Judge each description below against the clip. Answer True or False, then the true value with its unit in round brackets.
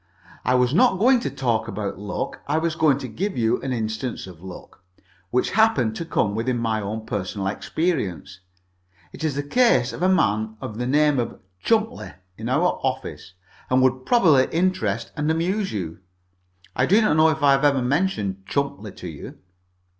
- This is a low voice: True (130 Hz)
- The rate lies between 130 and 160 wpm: False (185 wpm)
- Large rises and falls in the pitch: True (6.6 semitones)